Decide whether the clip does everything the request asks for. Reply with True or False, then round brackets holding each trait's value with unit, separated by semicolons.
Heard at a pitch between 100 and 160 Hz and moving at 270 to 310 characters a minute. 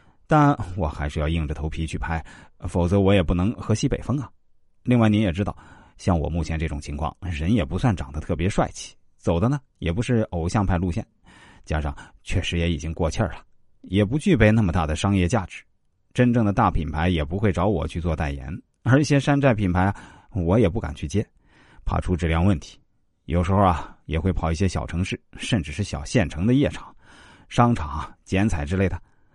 False (90 Hz; 290 characters per minute)